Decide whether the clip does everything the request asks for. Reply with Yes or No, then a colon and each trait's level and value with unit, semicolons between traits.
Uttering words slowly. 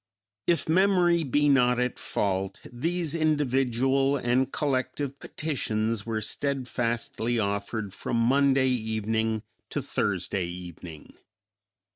Yes: slow, 100 wpm